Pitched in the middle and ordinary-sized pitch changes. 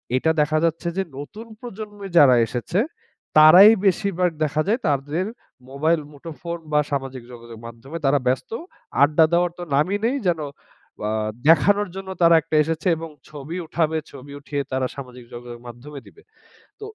Yes: medium, 155 Hz; average, 4.3 semitones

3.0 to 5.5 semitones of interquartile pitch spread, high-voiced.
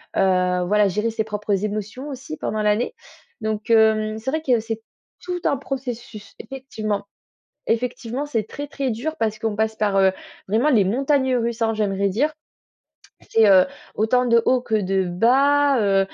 Yes: average, 3.6 semitones; high, 220 Hz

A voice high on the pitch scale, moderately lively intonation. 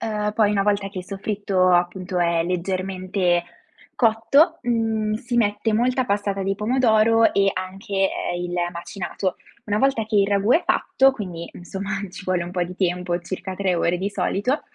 Yes: high, 195 Hz; average, 3.1 semitones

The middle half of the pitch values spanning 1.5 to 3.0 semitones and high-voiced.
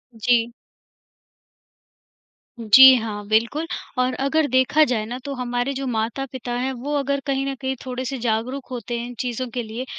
Yes: narrow, 2.4 semitones; very high, 250 Hz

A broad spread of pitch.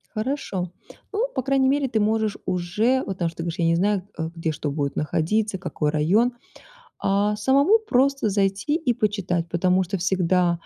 Yes: wide, 5.9 semitones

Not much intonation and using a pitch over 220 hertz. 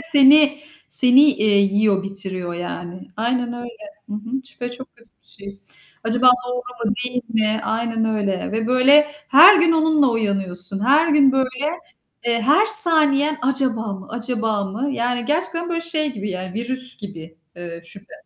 No: average, 5.1 semitones; high, 240 Hz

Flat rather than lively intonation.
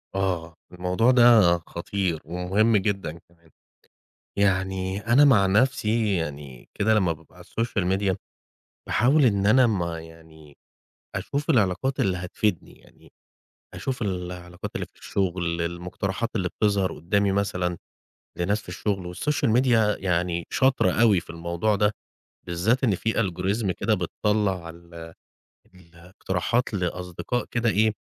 No: average, 3.8 semitones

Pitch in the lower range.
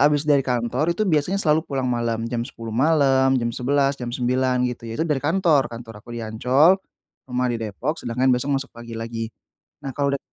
Yes: low, 130 Hz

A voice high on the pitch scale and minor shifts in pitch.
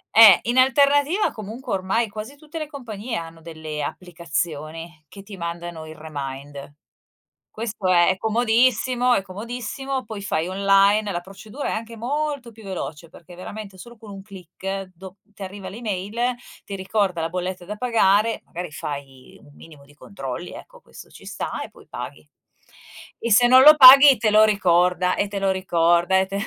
No: high, 195 Hz; average, 5.0 semitones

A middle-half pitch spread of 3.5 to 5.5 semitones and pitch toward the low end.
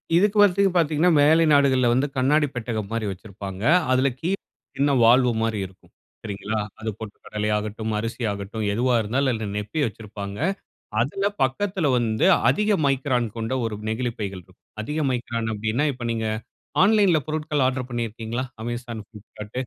Yes: average, 4.7 semitones; low, 120 Hz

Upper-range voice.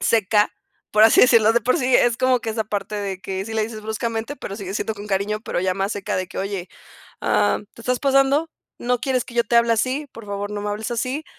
Yes: high, 220 Hz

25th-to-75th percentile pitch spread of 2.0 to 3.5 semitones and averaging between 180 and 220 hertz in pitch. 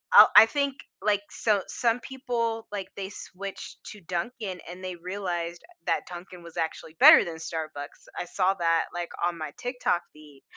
No: average, 4.0 semitones; medium, 185 Hz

